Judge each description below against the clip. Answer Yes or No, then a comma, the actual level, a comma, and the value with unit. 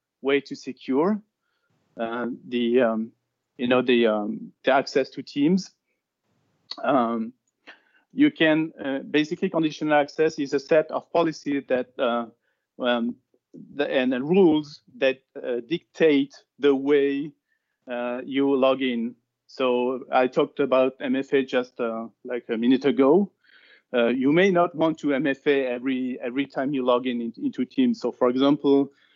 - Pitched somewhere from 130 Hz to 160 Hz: Yes, low, 135 Hz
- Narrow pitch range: No, average, 3.8 semitones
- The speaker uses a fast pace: No, average, 145 wpm